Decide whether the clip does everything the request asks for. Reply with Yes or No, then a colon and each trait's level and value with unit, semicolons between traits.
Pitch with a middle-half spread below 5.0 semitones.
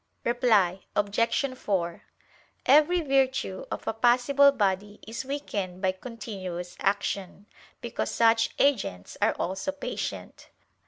No: wide, 5.5 semitones